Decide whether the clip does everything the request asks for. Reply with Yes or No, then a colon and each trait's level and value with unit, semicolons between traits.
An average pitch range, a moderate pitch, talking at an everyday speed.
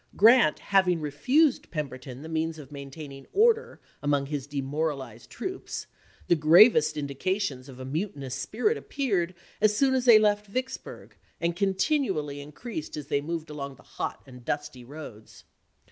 No: wide, 6.9 semitones; medium, 155 Hz; average, 155 wpm